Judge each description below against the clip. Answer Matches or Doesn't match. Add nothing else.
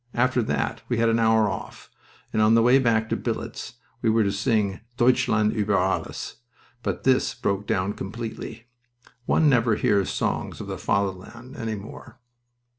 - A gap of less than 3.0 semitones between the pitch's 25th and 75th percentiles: Matches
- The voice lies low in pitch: Matches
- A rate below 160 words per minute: Doesn't match